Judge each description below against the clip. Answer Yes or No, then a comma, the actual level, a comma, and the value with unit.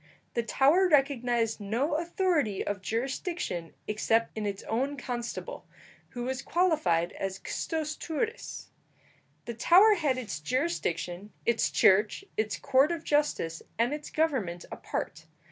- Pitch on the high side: Yes, high, 245 Hz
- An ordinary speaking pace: No, slow, 130 wpm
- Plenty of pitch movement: Yes, wide, 6.7 semitones